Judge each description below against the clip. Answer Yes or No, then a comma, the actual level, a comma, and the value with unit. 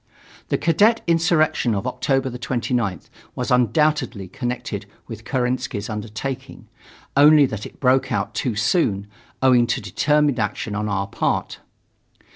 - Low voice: Yes, low, 125 Hz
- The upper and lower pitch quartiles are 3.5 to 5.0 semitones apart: Yes, average, 4.7 semitones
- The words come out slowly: Yes, slow, 125 wpm